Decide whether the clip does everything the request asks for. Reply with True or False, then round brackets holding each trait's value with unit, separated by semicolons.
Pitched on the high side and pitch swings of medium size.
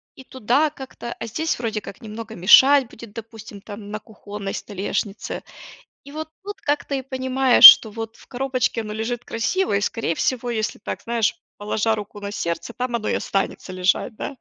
True (225 Hz; 3.8 semitones)